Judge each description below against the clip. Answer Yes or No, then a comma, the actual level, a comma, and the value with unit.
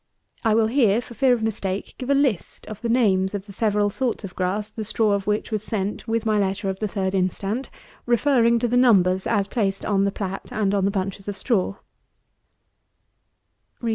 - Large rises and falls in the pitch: No, average, 2.8 semitones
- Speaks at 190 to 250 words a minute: Yes, average, 200 wpm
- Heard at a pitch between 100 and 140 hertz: No, high, 210 Hz